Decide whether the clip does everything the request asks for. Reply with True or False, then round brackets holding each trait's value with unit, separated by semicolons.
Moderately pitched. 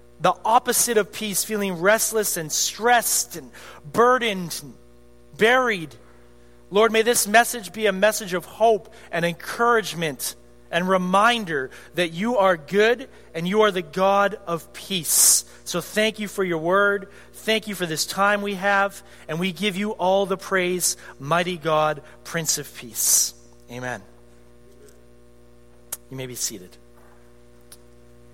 True (180 Hz)